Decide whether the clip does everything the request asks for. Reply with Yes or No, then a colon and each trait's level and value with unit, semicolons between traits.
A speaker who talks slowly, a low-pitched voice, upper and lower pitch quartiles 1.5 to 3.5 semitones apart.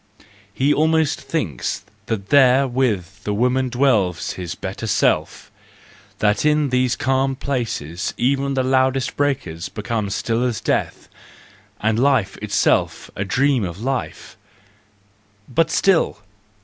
No: slow, 125 wpm; low, 125 Hz; average, 4.6 semitones